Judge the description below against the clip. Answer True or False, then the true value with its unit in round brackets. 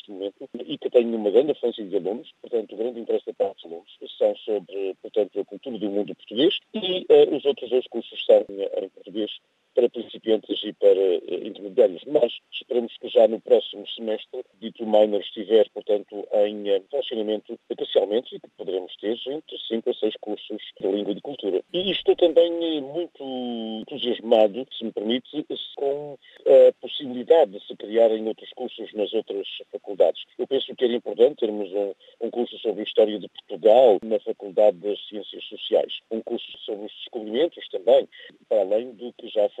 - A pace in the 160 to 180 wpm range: True (175 wpm)